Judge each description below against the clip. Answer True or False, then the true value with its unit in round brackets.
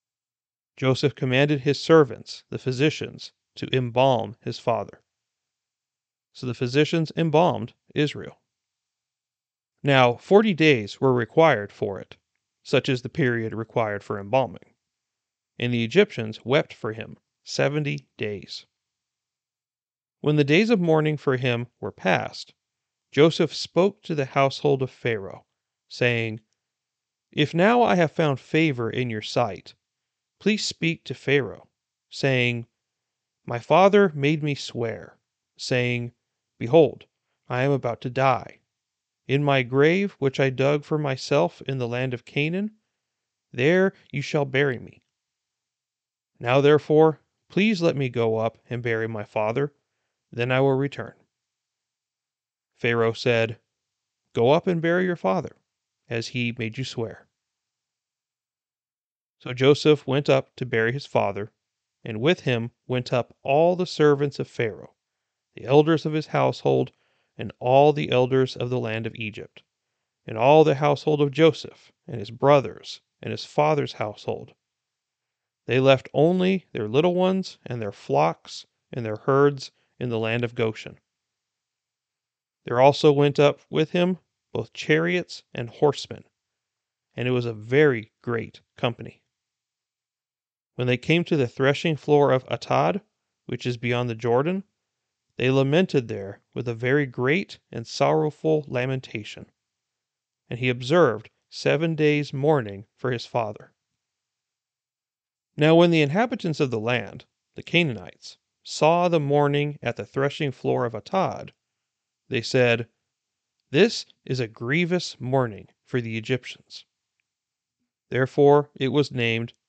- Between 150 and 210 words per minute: False (135 wpm)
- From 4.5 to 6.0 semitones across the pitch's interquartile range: False (3.9 semitones)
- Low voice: True (130 Hz)